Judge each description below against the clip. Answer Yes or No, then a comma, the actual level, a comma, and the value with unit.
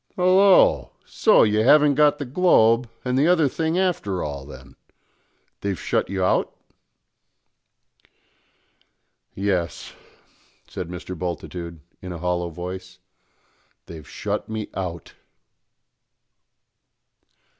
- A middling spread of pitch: No, wide, 8.6 semitones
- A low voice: Yes, very low, 95 Hz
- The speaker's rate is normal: No, slow, 100 wpm